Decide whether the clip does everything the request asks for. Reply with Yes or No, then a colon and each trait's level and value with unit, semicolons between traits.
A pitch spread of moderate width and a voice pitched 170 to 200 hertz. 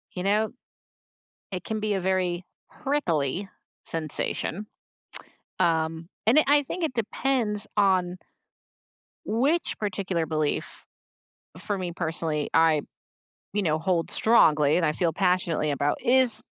Yes: average, 4.9 semitones; medium, 185 Hz